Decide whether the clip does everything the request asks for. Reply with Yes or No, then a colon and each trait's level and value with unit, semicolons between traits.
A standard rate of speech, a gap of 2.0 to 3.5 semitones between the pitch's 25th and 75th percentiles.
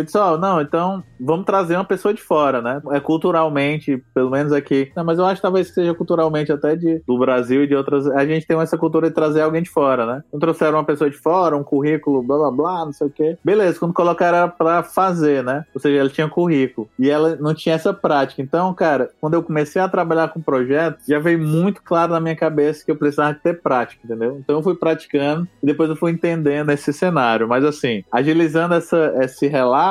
No: fast, 230 wpm; average, 2.9 semitones